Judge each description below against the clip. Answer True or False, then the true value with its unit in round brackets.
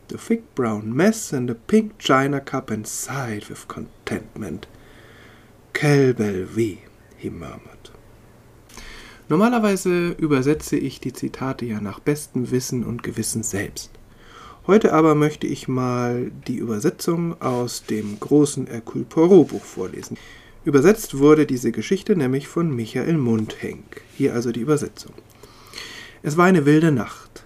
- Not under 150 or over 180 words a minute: False (125 wpm)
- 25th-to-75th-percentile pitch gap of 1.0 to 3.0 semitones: False (5.1 semitones)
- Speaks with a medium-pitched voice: False (125 Hz)